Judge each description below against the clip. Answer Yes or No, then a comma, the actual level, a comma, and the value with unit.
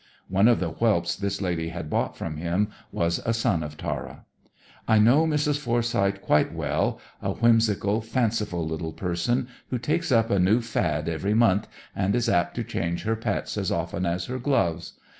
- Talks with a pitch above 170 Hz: No, low, 100 Hz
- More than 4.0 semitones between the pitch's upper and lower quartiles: Yes, average, 5.3 semitones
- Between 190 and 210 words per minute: No, average, 180 wpm